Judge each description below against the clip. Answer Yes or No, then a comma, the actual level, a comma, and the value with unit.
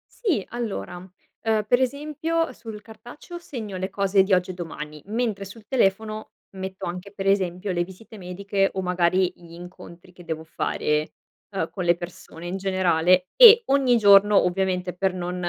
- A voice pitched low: No, high, 190 Hz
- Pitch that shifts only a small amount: No, average, 3.4 semitones